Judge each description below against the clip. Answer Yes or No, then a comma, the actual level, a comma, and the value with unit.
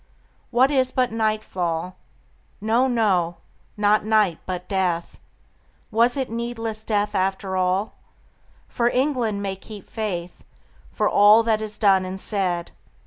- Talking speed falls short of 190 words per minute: Yes, slow, 135 wpm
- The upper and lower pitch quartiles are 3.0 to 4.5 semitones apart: Yes, average, 3.4 semitones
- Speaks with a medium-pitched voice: No, high, 210 Hz